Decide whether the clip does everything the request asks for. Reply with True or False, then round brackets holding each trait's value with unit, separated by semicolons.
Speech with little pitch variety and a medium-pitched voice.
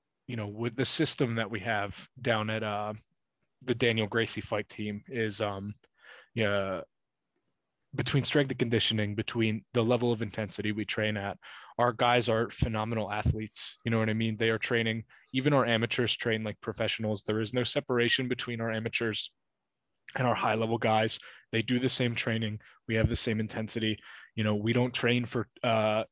False (2.0 semitones; 115 Hz)